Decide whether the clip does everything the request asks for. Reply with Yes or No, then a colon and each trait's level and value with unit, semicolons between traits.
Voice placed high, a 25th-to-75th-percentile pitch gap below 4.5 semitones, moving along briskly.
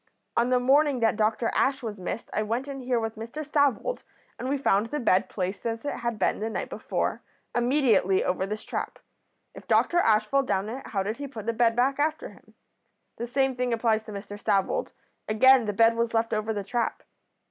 Yes: high, 230 Hz; average, 3.6 semitones; fast, 215 wpm